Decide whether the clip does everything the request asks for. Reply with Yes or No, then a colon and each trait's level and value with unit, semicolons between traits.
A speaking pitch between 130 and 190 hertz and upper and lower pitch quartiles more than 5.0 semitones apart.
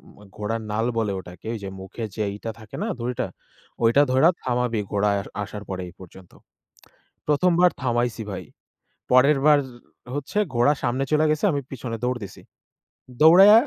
No: low, 120 Hz; wide, 5.4 semitones